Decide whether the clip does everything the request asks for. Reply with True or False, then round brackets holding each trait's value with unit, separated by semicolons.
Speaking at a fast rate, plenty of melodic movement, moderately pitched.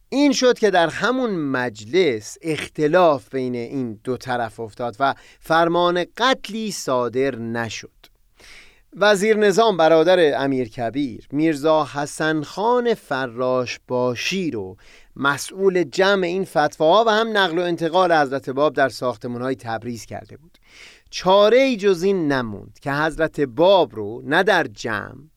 False (135 wpm; 7.0 semitones; 150 Hz)